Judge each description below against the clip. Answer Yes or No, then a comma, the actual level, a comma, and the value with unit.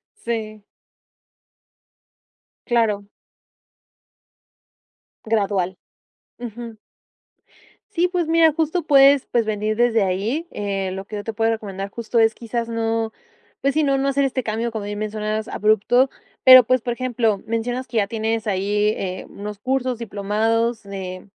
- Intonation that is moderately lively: Yes, average, 3.0 semitones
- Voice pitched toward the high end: Yes, high, 225 Hz